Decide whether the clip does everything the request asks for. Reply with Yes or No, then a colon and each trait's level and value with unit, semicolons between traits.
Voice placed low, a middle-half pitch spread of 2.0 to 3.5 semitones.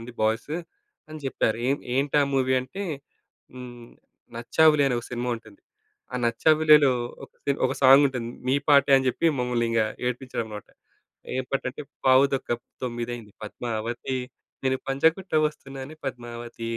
Yes: low, 130 Hz; average, 2.7 semitones